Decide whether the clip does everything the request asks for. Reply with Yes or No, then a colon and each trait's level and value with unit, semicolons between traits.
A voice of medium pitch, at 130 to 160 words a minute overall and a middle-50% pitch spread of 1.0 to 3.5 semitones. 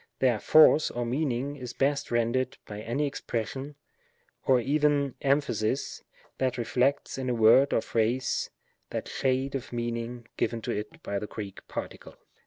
No: low, 125 Hz; average, 150 wpm; average, 2.9 semitones